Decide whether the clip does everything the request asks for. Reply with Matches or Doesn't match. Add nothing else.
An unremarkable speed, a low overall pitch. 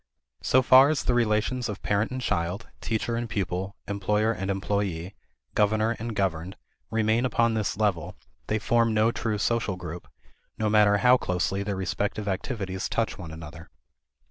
Matches